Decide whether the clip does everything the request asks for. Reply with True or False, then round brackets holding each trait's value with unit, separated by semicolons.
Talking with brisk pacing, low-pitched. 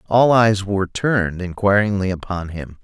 False (150 wpm; 100 Hz)